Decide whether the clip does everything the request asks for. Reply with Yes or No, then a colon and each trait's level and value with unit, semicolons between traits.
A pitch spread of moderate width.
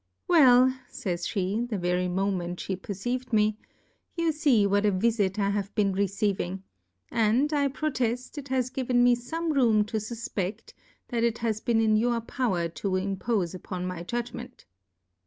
Yes: average, 4.1 semitones